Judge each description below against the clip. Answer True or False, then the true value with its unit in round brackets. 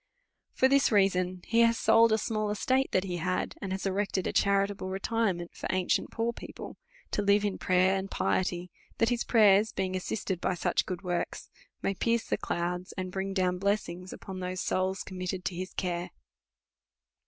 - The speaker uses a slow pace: False (190 wpm)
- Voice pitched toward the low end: False (190 Hz)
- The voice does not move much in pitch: True (2.3 semitones)